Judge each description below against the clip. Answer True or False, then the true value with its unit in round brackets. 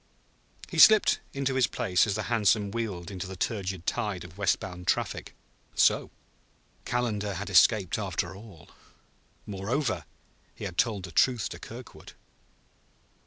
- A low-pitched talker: True (100 Hz)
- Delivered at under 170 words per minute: True (140 wpm)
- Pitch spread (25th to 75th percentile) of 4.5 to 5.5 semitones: False (3.6 semitones)